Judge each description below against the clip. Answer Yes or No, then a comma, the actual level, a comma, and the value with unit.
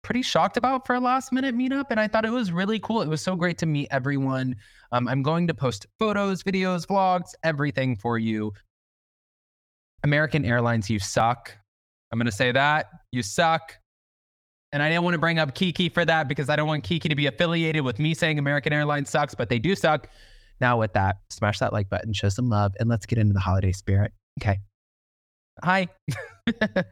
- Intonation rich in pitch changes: Yes, wide, 7.9 semitones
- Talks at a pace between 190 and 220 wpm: Yes, fast, 205 wpm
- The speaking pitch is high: No, medium, 145 Hz